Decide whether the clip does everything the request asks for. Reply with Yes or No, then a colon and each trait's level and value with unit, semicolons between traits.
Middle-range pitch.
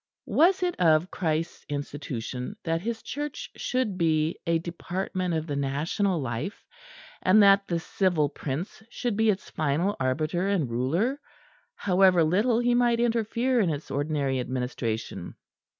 Yes: medium, 175 Hz